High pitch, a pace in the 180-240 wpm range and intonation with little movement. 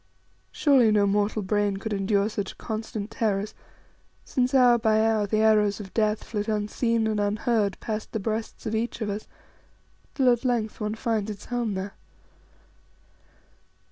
No: high, 215 Hz; average, 155 wpm; narrow, 1.5 semitones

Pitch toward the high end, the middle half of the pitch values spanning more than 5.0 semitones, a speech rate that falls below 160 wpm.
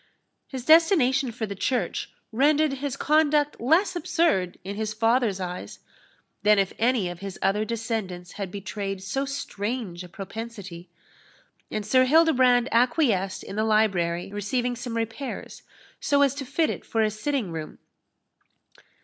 Yes: high, 225 Hz; wide, 5.4 semitones; average, 145 wpm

